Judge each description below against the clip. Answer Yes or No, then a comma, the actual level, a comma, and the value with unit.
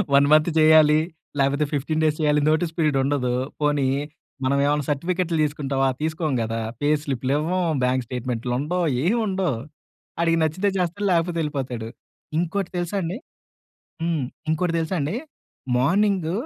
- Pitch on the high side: No, medium, 155 Hz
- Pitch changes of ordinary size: Yes, average, 3.6 semitones